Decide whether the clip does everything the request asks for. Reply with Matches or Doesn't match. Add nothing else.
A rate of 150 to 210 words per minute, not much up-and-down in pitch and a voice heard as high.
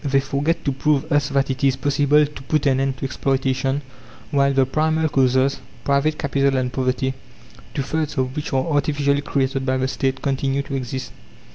Doesn't match